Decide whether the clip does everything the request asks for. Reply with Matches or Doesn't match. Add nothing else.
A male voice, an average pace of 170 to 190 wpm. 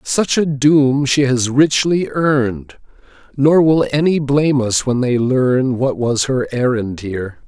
Doesn't match